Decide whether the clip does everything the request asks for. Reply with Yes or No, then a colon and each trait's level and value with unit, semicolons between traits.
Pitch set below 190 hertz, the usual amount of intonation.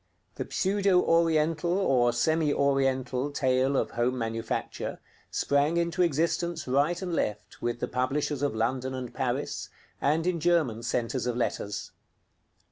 Yes: medium, 140 Hz; average, 4.9 semitones